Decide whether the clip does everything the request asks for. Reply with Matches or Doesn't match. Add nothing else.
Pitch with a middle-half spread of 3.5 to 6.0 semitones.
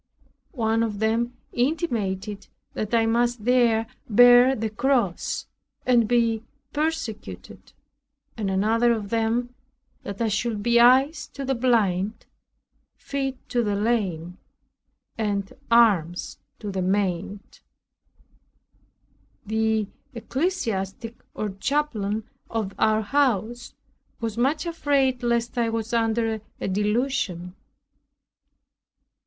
Doesn't match